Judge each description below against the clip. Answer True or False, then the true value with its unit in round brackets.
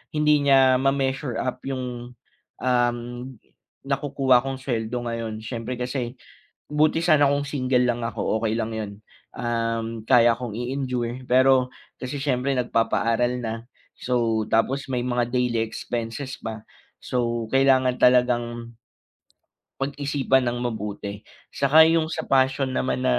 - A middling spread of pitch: False (2.3 semitones)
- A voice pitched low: True (125 Hz)